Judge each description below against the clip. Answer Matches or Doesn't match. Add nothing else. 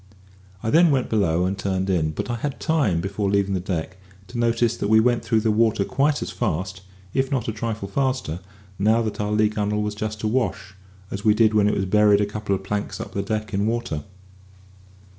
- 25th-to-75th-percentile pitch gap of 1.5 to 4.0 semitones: Matches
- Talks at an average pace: Doesn't match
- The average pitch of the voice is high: Doesn't match